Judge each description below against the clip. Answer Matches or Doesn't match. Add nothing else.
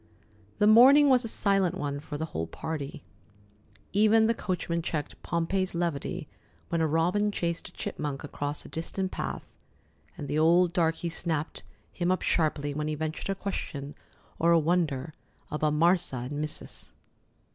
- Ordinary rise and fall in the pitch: Matches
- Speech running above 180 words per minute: Doesn't match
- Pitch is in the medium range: Matches